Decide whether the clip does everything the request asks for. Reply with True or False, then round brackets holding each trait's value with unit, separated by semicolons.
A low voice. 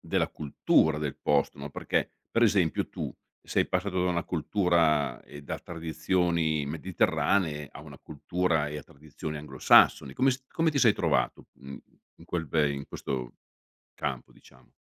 True (80 Hz)